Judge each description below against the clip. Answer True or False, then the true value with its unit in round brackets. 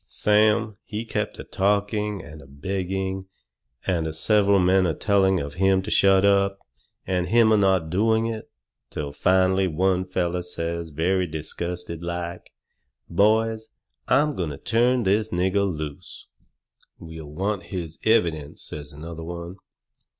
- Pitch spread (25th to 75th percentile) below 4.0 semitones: True (3.3 semitones)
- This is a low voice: True (95 Hz)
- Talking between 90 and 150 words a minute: True (140 wpm)